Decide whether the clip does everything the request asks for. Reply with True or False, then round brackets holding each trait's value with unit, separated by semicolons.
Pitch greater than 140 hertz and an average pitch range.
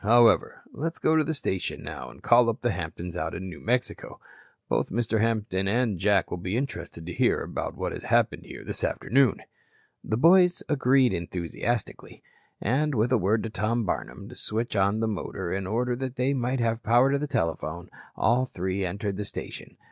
False (115 Hz; 4.7 semitones)